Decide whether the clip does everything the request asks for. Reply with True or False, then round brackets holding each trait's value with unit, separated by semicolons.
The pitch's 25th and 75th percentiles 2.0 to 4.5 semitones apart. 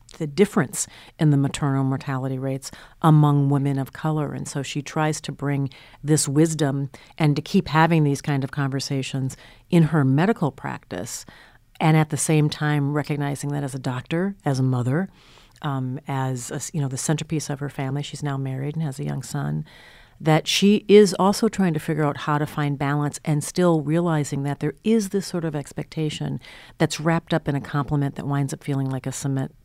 True (2.5 semitones)